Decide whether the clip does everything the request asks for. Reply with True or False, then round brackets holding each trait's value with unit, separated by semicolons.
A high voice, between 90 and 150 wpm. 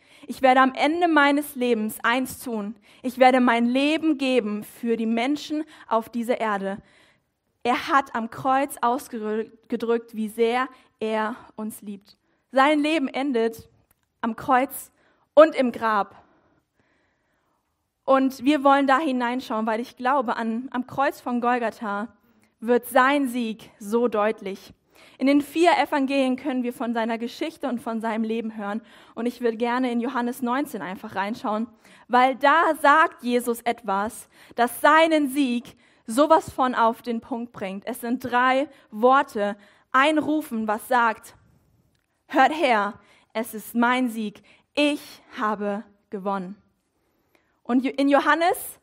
True (245 Hz; 140 wpm)